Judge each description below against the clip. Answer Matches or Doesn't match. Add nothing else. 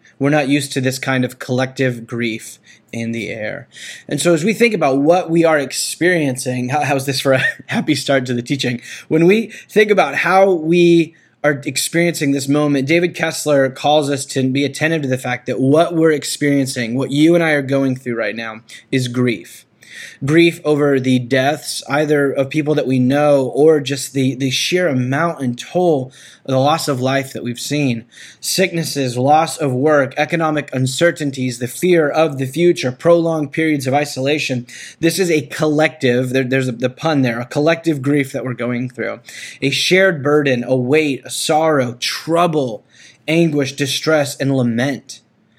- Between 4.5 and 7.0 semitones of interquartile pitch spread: Doesn't match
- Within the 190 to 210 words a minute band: Doesn't match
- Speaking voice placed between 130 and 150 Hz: Matches